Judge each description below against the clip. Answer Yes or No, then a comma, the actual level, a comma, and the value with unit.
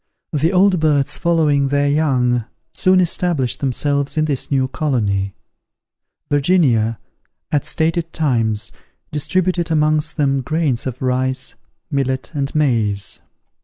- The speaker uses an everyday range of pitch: Yes, average, 3.5 semitones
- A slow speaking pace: Yes, slow, 115 wpm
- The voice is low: No, medium, 145 Hz